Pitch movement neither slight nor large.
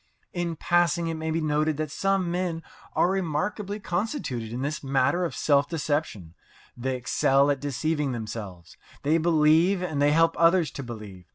Yes: average, 4.2 semitones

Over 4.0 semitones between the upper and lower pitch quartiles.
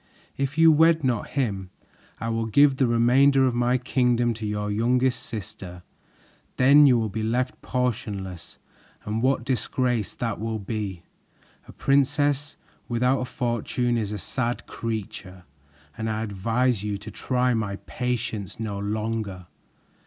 No: average, 3.2 semitones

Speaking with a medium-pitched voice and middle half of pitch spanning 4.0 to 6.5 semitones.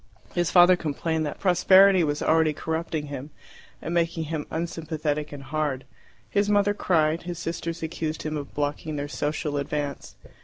No: medium, 160 Hz; narrow, 2.5 semitones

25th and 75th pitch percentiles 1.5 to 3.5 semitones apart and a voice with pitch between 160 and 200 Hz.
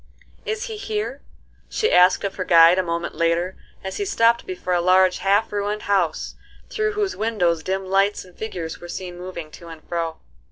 No: average, 4.1 semitones; medium, 185 Hz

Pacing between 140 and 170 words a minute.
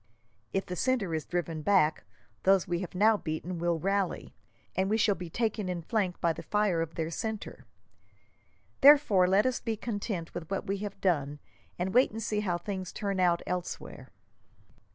No: average, 180 wpm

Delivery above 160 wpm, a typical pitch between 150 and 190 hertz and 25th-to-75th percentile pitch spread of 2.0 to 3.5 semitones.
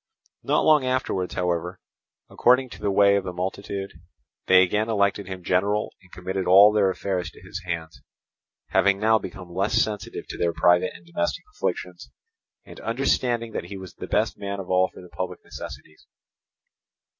No: average, 170 wpm; very low, 95 Hz; narrow, 2.6 semitones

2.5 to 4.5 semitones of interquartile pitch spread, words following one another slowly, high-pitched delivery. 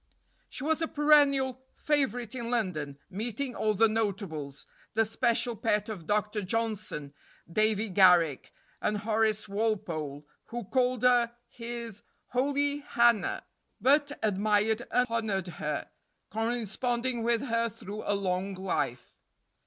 Yes: average, 3.6 semitones; slow, 120 wpm; high, 220 Hz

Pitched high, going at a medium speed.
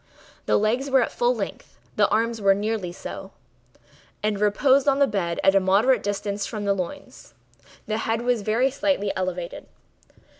Yes: high, 215 Hz; average, 165 wpm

